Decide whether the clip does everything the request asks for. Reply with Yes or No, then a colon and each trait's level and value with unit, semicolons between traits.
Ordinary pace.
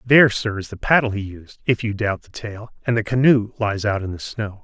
No: fast, 260 wpm